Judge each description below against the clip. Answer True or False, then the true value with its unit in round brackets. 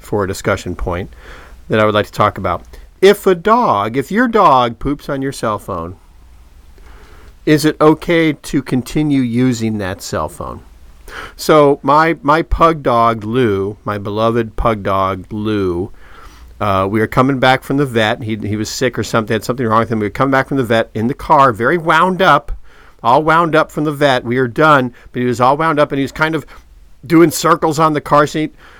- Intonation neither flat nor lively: False (6.7 semitones)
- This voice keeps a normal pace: False (210 wpm)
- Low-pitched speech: True (125 Hz)